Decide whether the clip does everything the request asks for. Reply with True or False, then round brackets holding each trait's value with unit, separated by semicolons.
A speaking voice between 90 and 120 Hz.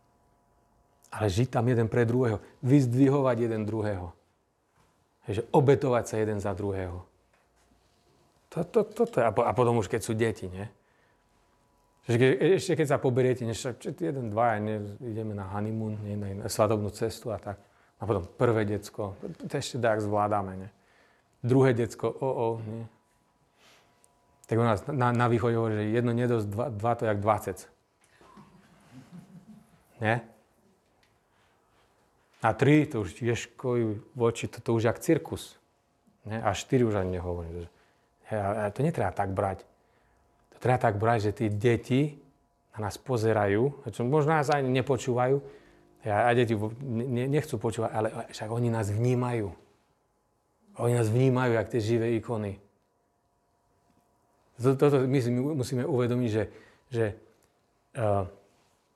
True (115 Hz)